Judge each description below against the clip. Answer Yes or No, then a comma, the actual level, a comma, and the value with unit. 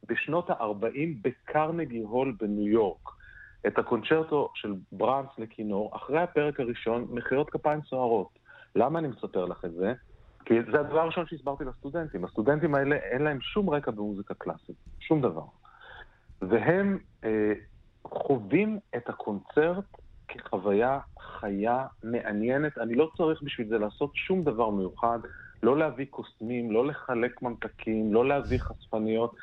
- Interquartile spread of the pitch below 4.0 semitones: No, wide, 5.4 semitones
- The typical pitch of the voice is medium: No, low, 125 Hz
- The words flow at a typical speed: Yes, average, 135 wpm